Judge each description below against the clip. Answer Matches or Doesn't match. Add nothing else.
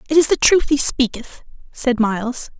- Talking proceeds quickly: Doesn't match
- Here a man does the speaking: Doesn't match